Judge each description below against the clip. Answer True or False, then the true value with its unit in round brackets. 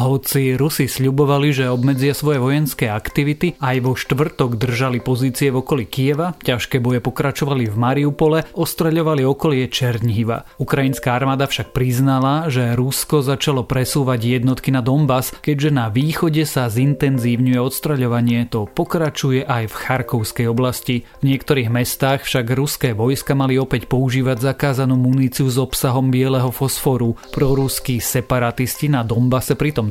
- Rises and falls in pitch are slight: True (2.2 semitones)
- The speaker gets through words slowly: False (135 wpm)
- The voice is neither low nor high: False (130 Hz)